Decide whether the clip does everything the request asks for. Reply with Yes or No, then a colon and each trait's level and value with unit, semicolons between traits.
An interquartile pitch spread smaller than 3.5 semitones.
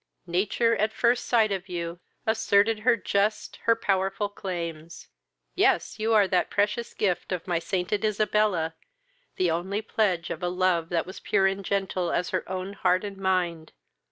Yes: average, 3.0 semitones